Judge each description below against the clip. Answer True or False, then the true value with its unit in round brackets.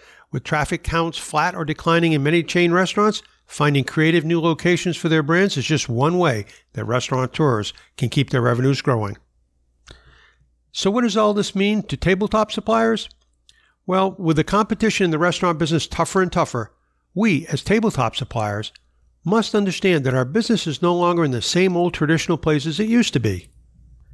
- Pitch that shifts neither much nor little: False (6.7 semitones)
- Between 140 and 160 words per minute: False (175 wpm)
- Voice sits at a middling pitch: True (160 Hz)